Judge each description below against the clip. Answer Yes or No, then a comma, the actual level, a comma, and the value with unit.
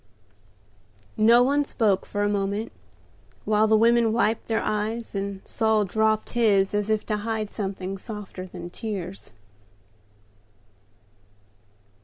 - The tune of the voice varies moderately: No, narrow, 2.0 semitones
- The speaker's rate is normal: No, slow, 120 wpm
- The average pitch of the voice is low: No, high, 215 Hz